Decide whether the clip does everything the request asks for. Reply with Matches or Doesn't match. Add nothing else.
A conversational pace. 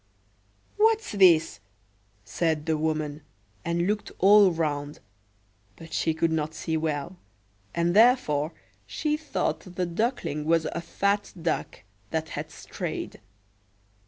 Doesn't match